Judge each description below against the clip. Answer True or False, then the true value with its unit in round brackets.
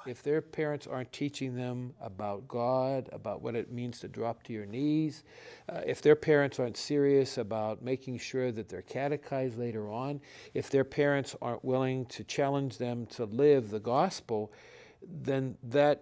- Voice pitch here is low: True (130 Hz)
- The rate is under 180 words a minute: True (170 wpm)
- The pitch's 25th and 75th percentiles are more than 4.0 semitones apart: False (2.9 semitones)